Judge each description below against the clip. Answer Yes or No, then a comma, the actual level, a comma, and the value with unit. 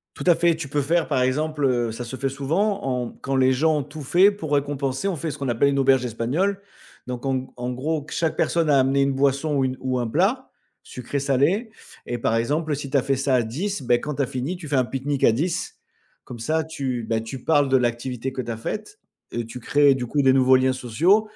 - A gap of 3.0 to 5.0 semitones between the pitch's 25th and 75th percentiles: Yes, average, 3.6 semitones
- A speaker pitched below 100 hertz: No, low, 135 Hz